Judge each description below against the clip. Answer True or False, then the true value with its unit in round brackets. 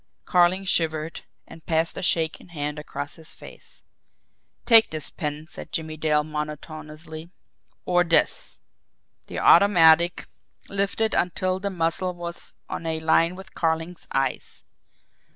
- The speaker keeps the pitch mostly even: True (2.3 semitones)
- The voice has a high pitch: False (165 Hz)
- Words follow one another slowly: True (125 wpm)